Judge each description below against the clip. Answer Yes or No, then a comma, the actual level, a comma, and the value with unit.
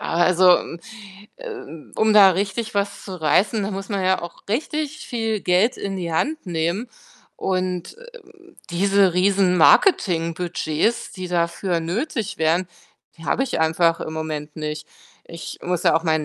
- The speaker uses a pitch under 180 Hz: No, medium, 185 Hz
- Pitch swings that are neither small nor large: Yes, average, 3.8 semitones